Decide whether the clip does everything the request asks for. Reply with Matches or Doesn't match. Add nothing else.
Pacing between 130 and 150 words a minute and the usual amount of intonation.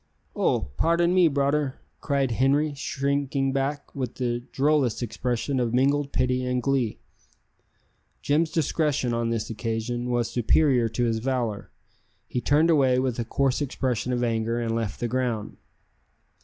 Matches